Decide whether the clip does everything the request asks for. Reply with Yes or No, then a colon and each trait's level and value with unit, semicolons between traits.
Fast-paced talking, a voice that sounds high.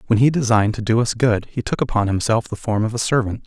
No: fast, 275 wpm; low, 115 Hz